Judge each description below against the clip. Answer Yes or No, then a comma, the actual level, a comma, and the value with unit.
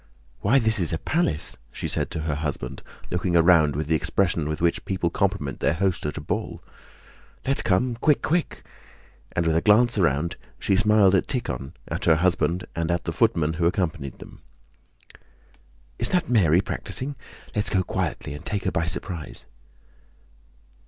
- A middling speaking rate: Yes, average, 170 wpm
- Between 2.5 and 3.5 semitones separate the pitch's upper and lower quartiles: No, average, 4.5 semitones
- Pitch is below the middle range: Yes, very low, 85 Hz